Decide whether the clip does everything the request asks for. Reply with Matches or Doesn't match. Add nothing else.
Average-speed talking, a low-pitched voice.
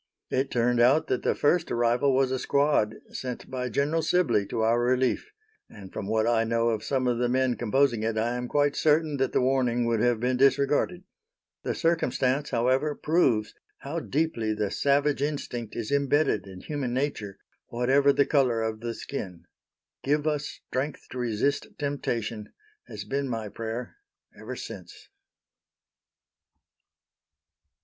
Matches